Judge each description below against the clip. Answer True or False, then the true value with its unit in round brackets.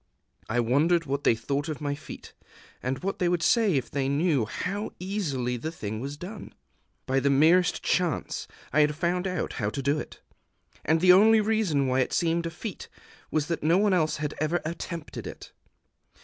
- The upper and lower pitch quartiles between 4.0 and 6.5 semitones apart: True (4.4 semitones)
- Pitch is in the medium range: True (155 Hz)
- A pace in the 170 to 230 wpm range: True (190 wpm)